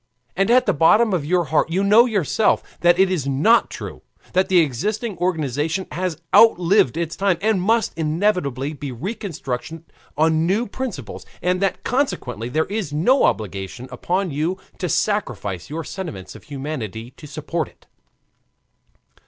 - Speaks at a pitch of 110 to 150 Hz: No, medium, 170 Hz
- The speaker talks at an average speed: Yes, average, 155 wpm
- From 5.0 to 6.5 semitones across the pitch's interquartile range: Yes, wide, 5.6 semitones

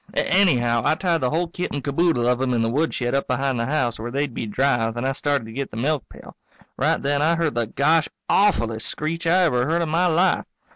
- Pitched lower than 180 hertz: Yes, medium, 140 Hz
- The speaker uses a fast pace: Yes, fast, 235 wpm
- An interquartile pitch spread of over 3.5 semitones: Yes, average, 5.3 semitones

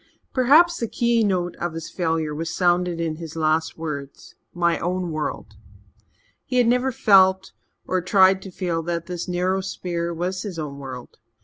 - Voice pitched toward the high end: No, medium, 175 Hz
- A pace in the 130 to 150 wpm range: No, average, 165 wpm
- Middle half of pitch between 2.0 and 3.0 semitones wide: Yes, narrow, 2.6 semitones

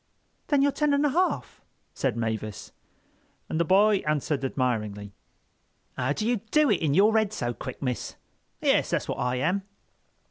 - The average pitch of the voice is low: No, medium, 155 Hz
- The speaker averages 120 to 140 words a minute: No, average, 170 wpm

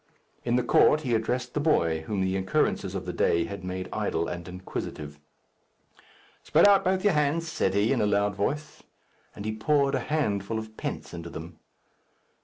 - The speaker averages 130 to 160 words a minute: No, average, 185 wpm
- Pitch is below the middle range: Yes, low, 110 Hz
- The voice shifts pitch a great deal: Yes, wide, 7.9 semitones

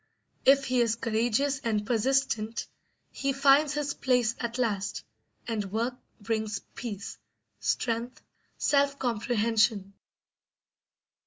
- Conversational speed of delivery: No, slow, 100 wpm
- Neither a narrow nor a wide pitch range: Yes, average, 3.7 semitones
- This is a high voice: Yes, high, 235 Hz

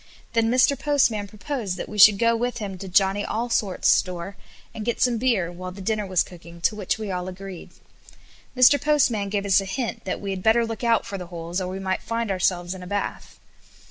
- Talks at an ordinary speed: No, fast, 220 wpm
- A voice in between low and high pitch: No, high, 200 Hz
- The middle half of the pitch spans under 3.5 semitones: No, average, 3.8 semitones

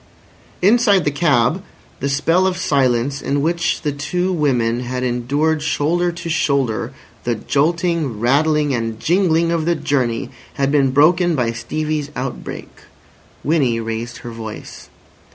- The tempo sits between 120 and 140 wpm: Yes, slow, 135 wpm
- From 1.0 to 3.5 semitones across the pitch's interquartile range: No, average, 5.3 semitones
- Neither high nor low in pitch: Yes, medium, 145 Hz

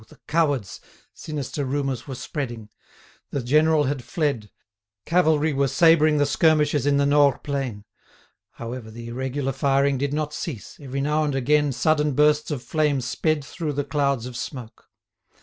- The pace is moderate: Yes, average, 150 wpm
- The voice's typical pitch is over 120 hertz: Yes, medium, 140 Hz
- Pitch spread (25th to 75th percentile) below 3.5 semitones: Yes, narrow, 2.6 semitones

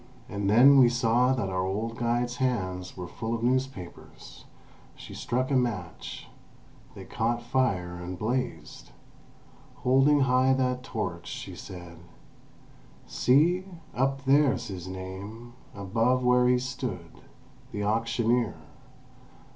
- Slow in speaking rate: Yes, slow, 120 wpm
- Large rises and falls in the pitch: No, average, 4.7 semitones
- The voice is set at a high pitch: No, low, 120 Hz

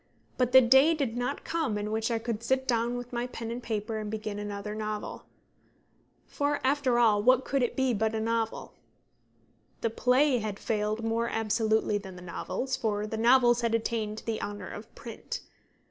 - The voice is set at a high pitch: Yes, high, 230 Hz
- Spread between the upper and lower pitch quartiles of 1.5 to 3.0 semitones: Yes, narrow, 2.5 semitones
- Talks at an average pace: Yes, average, 180 wpm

